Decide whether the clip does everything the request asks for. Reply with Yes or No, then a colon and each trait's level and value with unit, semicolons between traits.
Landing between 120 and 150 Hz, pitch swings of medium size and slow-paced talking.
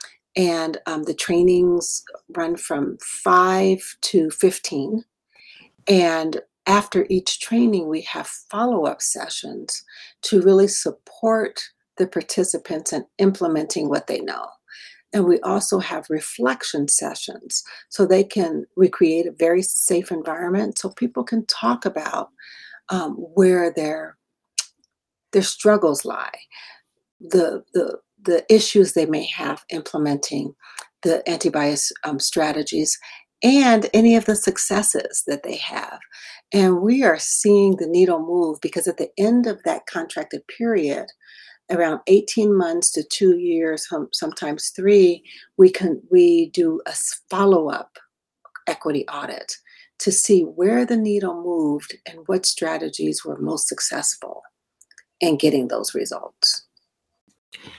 No: medium, 185 Hz; average, 4.5 semitones; slow, 125 wpm